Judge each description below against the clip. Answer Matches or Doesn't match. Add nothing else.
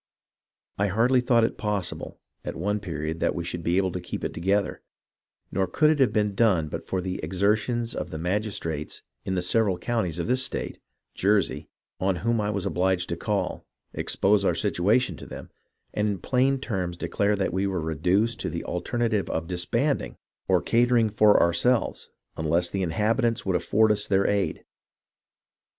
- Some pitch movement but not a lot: Matches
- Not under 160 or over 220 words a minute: Matches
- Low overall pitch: Matches